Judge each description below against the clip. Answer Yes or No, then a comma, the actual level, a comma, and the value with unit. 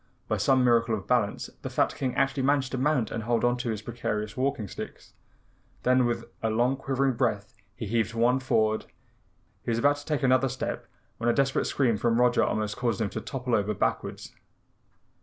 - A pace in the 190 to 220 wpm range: Yes, average, 195 wpm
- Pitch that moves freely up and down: No, average, 2.9 semitones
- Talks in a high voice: No, low, 120 Hz